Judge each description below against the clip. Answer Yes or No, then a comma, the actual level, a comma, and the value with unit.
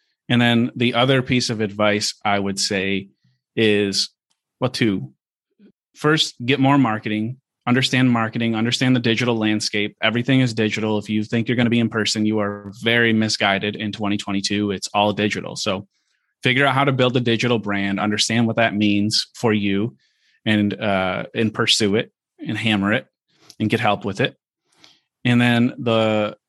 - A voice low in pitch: Yes, low, 110 Hz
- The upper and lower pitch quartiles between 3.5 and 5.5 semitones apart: No, narrow, 2.6 semitones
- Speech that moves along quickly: No, average, 170 wpm